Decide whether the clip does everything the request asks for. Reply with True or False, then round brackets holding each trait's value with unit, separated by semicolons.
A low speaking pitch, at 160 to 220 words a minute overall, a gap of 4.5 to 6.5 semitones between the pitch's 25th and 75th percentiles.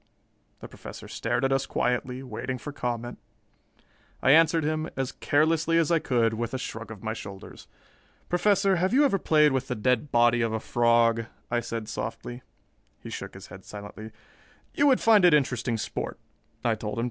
True (125 Hz; 180 wpm; 5.4 semitones)